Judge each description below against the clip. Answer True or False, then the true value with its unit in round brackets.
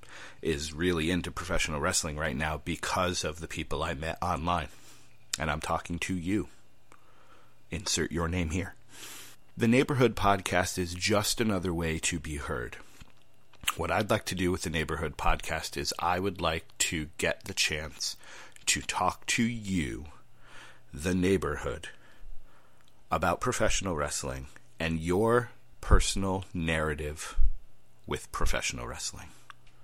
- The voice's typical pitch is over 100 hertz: False (90 Hz)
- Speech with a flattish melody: False (3.1 semitones)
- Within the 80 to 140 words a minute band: True (135 wpm)